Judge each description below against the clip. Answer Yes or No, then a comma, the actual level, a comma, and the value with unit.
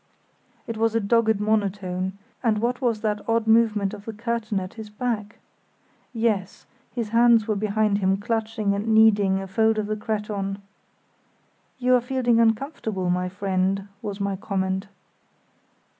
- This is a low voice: No, high, 215 Hz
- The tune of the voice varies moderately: No, narrow, 2.3 semitones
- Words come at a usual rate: Yes, average, 150 wpm